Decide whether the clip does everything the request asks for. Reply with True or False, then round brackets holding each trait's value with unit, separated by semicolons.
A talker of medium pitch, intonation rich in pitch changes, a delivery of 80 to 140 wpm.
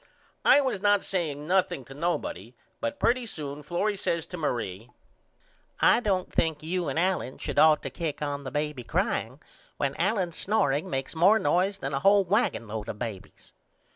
False (165 Hz; 5.8 semitones; 170 wpm)